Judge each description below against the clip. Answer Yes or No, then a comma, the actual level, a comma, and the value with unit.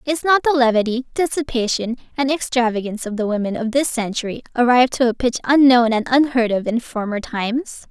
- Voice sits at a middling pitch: No, high, 245 Hz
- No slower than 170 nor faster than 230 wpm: Yes, average, 180 wpm